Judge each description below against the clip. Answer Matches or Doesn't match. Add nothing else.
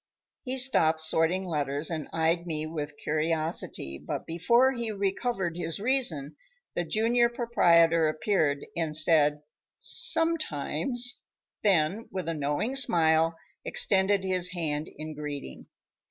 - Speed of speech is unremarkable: Doesn't match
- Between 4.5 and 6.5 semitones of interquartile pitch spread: Matches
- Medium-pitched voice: Matches